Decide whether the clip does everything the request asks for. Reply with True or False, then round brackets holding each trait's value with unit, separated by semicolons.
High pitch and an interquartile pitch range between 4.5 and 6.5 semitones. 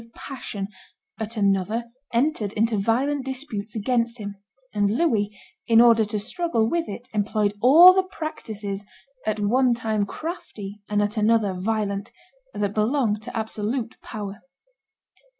False (220 Hz; 3.2 semitones)